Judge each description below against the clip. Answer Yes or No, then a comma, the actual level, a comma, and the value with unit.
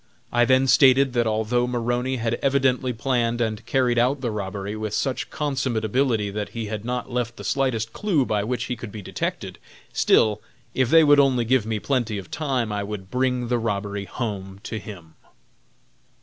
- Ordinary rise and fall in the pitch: Yes, average, 3.3 semitones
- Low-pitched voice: Yes, low, 120 Hz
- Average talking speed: Yes, average, 185 wpm